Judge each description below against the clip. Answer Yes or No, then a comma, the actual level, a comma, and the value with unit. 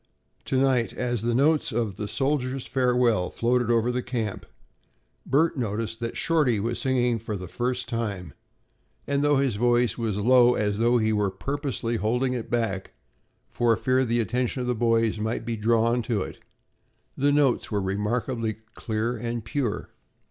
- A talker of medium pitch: No, low, 120 Hz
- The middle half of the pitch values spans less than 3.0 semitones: Yes, narrow, 2.4 semitones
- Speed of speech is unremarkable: Yes, average, 165 wpm